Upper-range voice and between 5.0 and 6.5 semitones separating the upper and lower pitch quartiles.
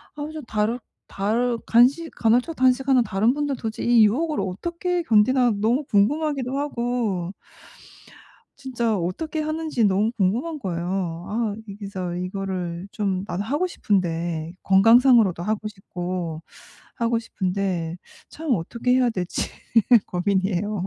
Yes: high, 215 Hz; wide, 5.5 semitones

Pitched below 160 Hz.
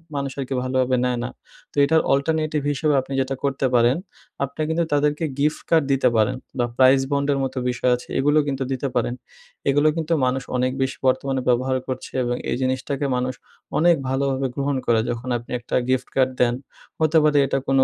Yes: low, 135 Hz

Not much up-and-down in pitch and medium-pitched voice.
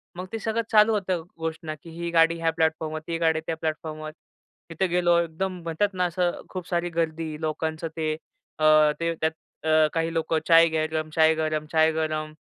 Yes: narrow, 1.4 semitones; medium, 165 Hz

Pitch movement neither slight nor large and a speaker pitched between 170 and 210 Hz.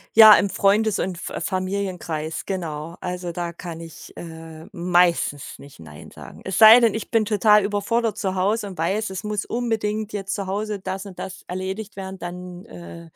Yes: average, 3.3 semitones; high, 190 Hz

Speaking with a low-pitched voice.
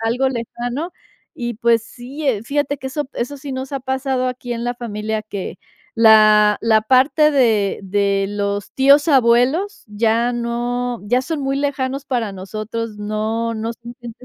No: high, 240 Hz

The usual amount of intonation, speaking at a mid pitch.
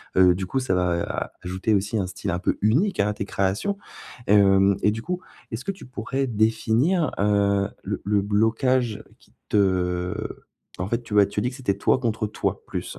No: average, 3.5 semitones; low, 105 Hz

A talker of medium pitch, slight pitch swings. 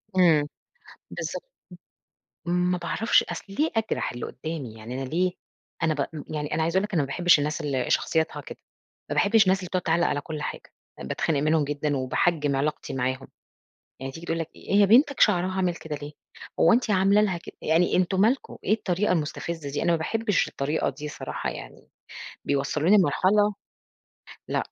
No: medium, 165 Hz; average, 4.3 semitones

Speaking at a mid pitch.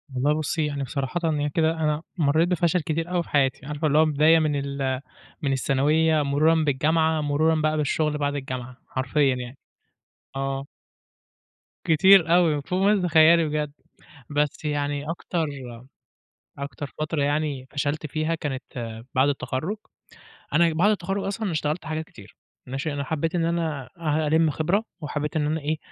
Yes: medium, 150 Hz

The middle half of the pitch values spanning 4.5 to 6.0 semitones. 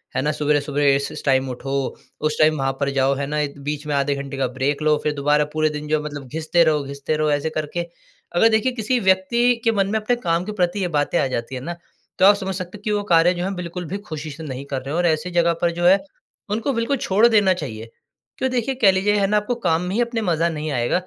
Yes: average, 5.1 semitones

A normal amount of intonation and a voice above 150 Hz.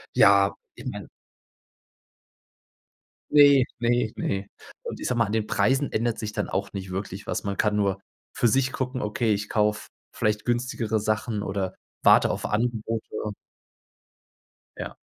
No: average, 3.0 semitones; low, 110 Hz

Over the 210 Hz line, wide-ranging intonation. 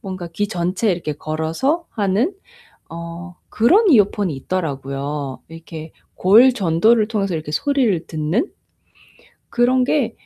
No: medium, 185 Hz; wide, 6.4 semitones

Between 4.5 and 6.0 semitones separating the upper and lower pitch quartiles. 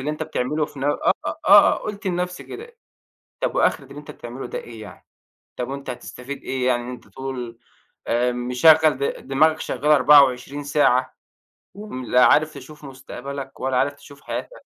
No: average, 3.2 semitones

